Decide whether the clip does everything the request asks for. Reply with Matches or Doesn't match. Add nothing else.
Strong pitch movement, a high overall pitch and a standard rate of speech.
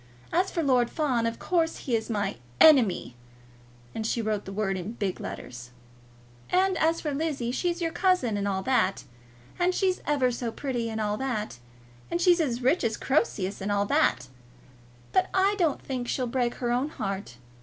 Matches